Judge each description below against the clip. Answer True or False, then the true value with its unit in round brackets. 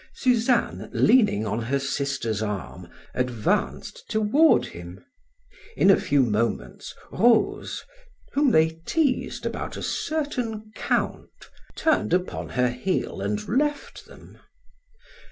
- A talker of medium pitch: True (165 Hz)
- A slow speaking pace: True (110 wpm)